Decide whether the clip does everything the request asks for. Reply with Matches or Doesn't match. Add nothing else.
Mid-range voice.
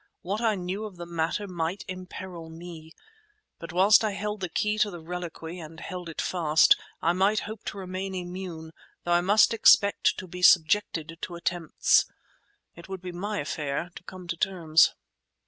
Matches